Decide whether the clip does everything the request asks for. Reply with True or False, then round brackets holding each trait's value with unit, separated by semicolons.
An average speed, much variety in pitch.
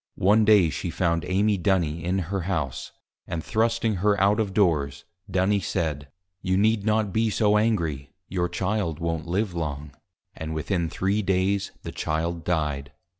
False (160 wpm; 4.1 semitones)